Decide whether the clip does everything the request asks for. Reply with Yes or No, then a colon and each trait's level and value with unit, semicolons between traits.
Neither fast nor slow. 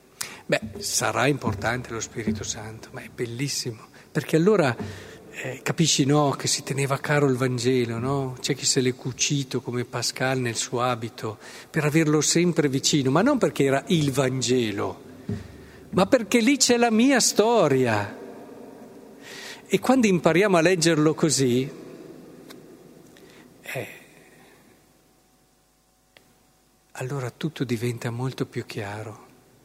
Yes: average, 125 wpm